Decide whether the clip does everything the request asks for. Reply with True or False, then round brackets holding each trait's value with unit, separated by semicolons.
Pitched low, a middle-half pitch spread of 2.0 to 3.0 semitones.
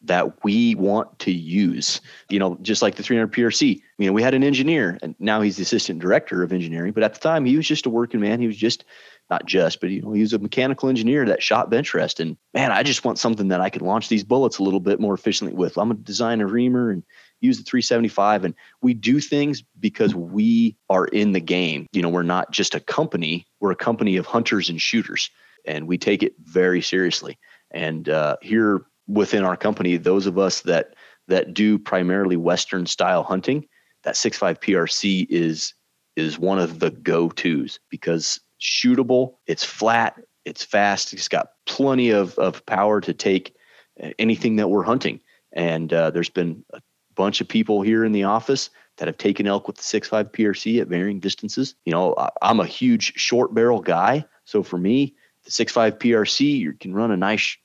False (105 Hz; 4.6 semitones)